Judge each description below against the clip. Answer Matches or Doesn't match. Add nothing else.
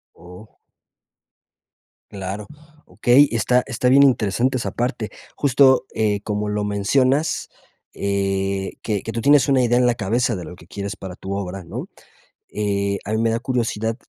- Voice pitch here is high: Doesn't match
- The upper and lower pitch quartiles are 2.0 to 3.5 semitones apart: Doesn't match